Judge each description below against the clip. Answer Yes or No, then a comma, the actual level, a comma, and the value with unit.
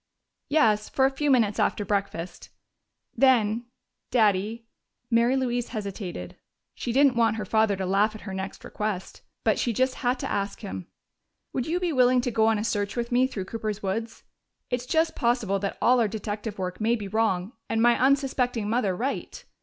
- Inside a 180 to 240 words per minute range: Yes, average, 185 wpm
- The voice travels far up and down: No, average, 3.4 semitones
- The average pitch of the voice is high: Yes, high, 225 Hz